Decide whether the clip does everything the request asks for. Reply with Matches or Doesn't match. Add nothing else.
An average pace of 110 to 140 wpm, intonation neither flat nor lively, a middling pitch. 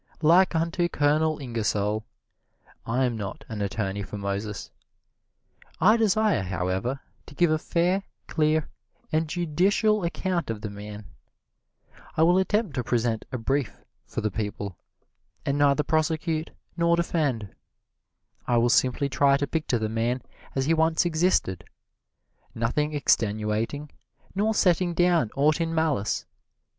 Doesn't match